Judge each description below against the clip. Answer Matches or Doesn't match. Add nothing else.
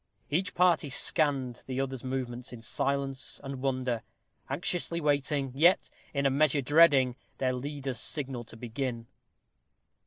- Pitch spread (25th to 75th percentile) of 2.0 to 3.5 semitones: Matches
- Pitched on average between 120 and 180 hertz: Matches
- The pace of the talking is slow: Matches